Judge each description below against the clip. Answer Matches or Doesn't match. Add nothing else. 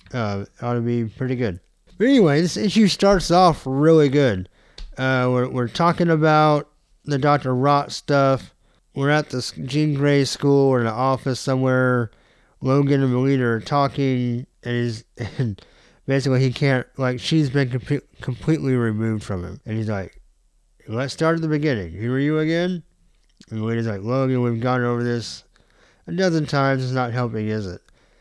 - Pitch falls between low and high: Doesn't match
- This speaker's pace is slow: Doesn't match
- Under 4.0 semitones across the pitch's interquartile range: Matches